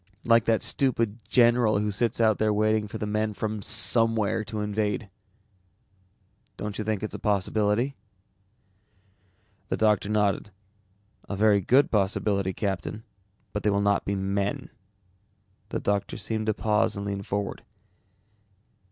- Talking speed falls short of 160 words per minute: Yes, average, 140 wpm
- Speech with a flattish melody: Yes, narrow, 1.4 semitones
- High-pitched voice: No, low, 105 Hz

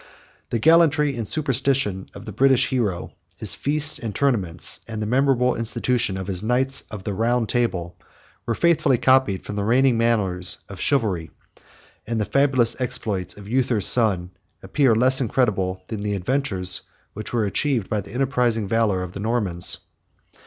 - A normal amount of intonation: Yes, average, 4.8 semitones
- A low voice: Yes, low, 115 Hz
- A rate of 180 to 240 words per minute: No, average, 160 wpm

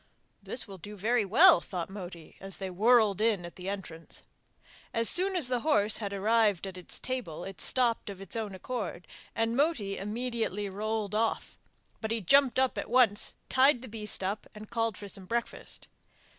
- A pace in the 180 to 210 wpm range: Yes, average, 185 wpm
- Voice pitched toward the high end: Yes, high, 215 Hz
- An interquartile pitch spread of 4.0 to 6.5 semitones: No, average, 3.5 semitones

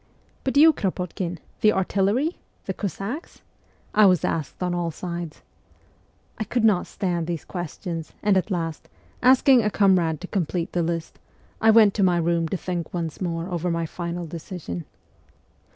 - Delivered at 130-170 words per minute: Yes, average, 165 wpm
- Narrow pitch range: No, average, 3.2 semitones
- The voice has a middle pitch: Yes, medium, 180 Hz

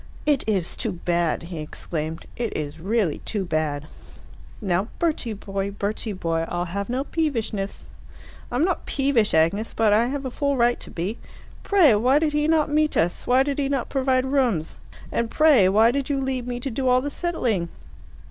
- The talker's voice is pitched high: Yes, high, 235 Hz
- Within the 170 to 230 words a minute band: Yes, average, 190 wpm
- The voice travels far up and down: Yes, wide, 6.6 semitones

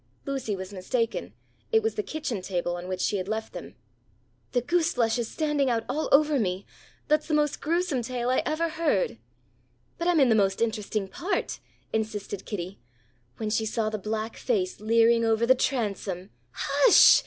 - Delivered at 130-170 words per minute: No, average, 180 wpm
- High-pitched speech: Yes, high, 230 Hz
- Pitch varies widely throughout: Yes, wide, 6.2 semitones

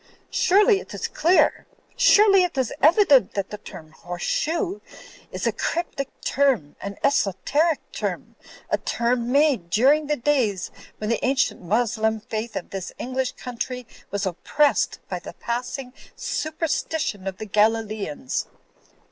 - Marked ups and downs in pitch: Yes, wide, 6.3 semitones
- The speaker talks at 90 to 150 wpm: Yes, average, 140 wpm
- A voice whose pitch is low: No, high, 245 Hz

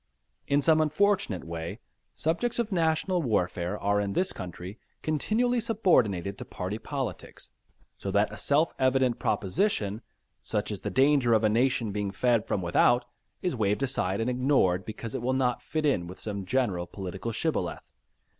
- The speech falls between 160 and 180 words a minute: Yes, average, 165 wpm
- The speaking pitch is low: Yes, low, 115 Hz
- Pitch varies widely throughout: Yes, wide, 7.1 semitones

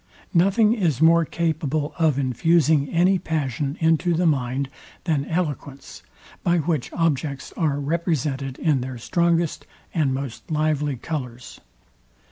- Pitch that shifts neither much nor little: Yes, average, 3.4 semitones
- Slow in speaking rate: Yes, slow, 120 wpm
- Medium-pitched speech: Yes, medium, 155 Hz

